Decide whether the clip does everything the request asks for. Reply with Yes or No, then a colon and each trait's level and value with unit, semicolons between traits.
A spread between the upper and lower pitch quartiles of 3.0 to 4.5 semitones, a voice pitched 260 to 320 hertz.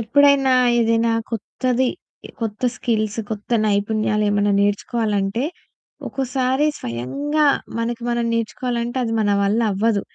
No: average, 3.3 semitones; high, 230 Hz